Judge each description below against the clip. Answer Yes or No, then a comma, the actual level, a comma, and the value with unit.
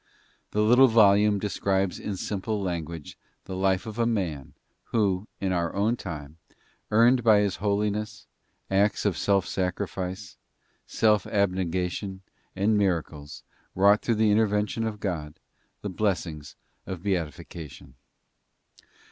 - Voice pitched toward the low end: Yes, low, 100 Hz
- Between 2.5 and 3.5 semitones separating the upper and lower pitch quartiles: Yes, average, 2.8 semitones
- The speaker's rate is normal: No, slow, 120 wpm